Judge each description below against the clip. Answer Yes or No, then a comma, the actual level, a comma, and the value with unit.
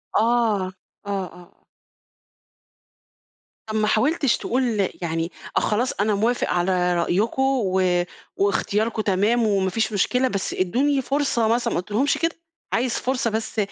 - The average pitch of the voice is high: Yes, high, 215 Hz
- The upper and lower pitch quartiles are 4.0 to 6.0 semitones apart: Yes, average, 4.3 semitones